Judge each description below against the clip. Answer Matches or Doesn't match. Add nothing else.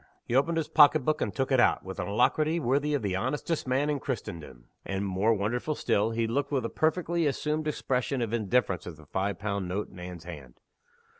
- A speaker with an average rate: Doesn't match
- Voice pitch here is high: Doesn't match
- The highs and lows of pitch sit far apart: Matches